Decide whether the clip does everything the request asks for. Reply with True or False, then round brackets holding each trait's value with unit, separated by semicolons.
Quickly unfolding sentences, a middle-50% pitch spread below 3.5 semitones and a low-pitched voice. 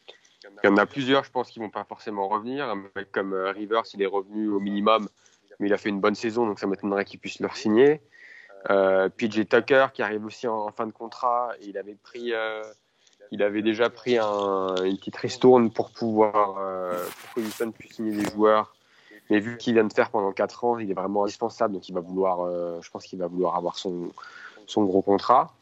True (230 wpm; 2.6 semitones; 105 Hz)